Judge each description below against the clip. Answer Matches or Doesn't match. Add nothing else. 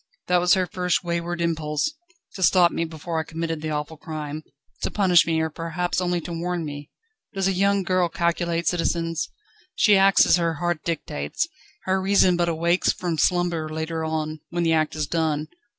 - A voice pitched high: Doesn't match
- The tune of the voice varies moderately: Doesn't match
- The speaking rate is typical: Matches